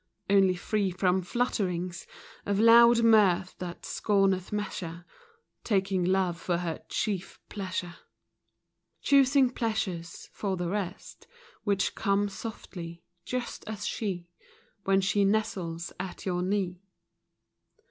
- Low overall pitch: No, high, 190 Hz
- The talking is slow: Yes, slow, 115 wpm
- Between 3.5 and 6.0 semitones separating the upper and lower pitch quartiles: No, average, 2.8 semitones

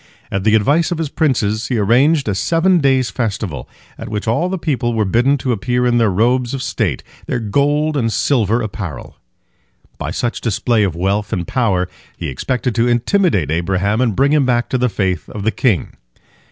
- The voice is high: No, low, 120 Hz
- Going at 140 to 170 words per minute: No, average, 195 wpm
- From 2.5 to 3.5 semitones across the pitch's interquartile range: No, average, 4.7 semitones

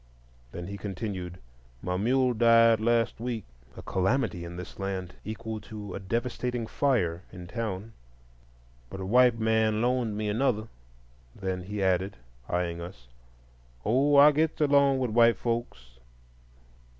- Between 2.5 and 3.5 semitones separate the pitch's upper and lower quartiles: No, average, 4.8 semitones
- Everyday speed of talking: No, slow, 130 wpm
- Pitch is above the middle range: No, low, 105 Hz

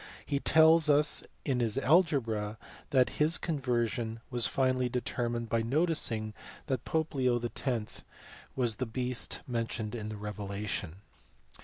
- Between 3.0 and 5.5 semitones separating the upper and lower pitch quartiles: Yes, average, 3.7 semitones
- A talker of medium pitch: No, low, 120 Hz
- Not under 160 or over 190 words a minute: No, average, 145 wpm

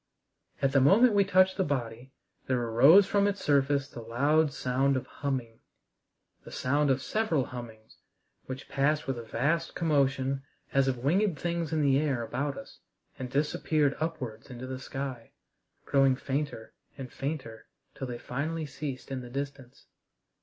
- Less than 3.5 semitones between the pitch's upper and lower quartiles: Yes, average, 3.1 semitones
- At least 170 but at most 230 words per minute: No, average, 160 wpm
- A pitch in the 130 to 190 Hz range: Yes, medium, 140 Hz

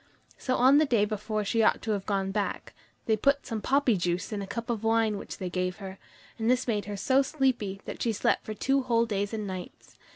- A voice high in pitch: Yes, high, 215 Hz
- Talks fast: Yes, fast, 235 wpm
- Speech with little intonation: No, average, 3.4 semitones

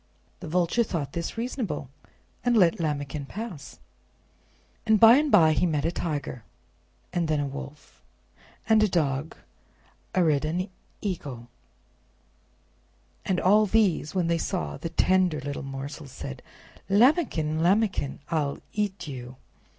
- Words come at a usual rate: No, slow, 130 wpm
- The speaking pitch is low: No, medium, 165 Hz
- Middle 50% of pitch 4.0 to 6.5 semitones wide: Yes, wide, 5.6 semitones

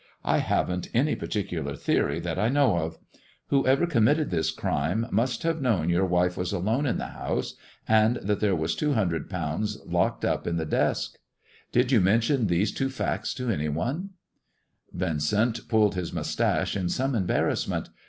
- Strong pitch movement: Yes, wide, 6.3 semitones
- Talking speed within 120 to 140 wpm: No, average, 170 wpm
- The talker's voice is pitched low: Yes, low, 105 Hz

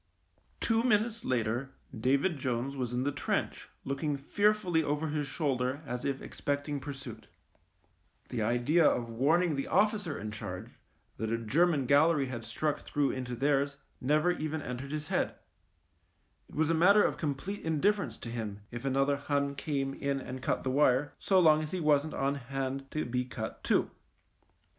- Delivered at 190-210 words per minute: No, average, 175 wpm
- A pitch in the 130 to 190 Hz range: Yes, medium, 140 Hz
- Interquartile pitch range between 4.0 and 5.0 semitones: No, average, 3.6 semitones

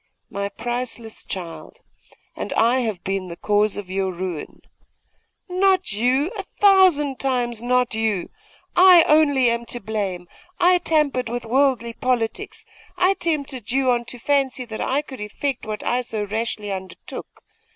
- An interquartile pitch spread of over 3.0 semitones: Yes, average, 5.0 semitones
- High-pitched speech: Yes, high, 240 Hz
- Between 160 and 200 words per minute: No, average, 150 wpm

